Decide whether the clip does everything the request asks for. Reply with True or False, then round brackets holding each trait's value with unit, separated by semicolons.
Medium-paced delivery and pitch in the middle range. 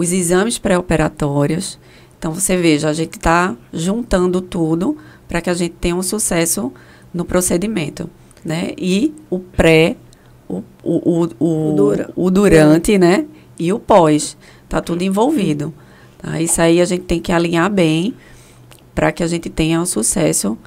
True (155 wpm; 170 Hz)